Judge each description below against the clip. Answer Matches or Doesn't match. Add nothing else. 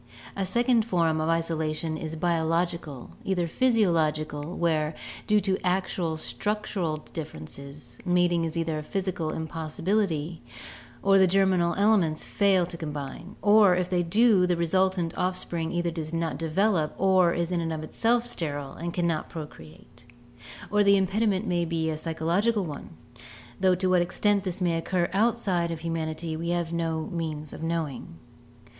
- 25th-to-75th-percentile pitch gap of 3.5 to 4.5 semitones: Doesn't match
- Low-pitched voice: Doesn't match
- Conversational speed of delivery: Matches